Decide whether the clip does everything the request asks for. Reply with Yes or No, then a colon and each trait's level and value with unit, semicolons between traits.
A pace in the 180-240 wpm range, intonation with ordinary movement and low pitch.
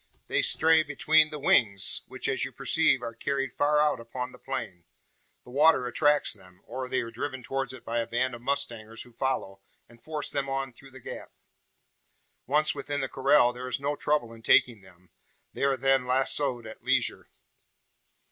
Yes: average, 185 wpm; average, 3.3 semitones; low, 130 Hz